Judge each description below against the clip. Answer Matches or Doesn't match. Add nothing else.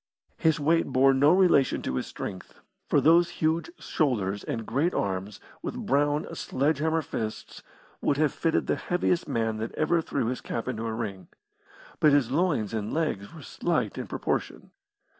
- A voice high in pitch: Doesn't match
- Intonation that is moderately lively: Doesn't match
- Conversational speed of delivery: Matches